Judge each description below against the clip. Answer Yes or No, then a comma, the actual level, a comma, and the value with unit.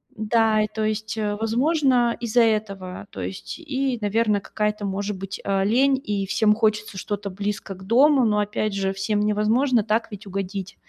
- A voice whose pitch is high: Yes, high, 210 Hz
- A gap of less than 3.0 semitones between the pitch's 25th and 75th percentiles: Yes, narrow, 2.4 semitones